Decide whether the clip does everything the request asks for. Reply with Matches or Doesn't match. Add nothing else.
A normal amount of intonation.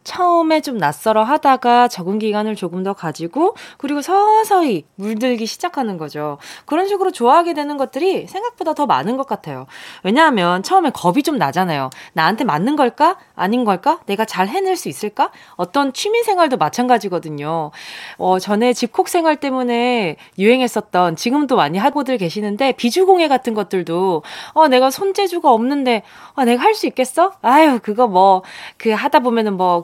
Doesn't match